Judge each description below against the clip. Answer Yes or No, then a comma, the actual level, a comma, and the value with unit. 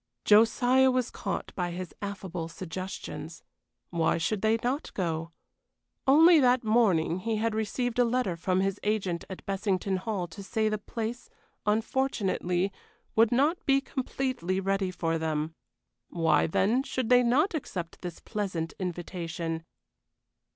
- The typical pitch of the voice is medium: No, high, 200 Hz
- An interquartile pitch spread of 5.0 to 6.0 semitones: Yes, wide, 5.5 semitones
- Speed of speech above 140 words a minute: No, slow, 135 wpm